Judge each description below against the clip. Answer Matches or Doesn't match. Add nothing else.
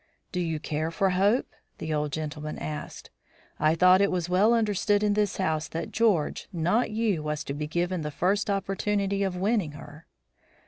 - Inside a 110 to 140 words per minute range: Doesn't match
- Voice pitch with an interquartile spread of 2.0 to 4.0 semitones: Doesn't match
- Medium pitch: Matches